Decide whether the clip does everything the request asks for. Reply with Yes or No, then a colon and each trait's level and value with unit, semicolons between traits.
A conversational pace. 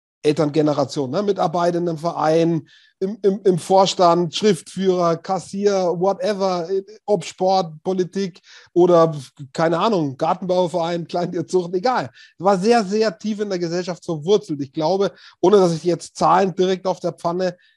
Yes: average, 140 wpm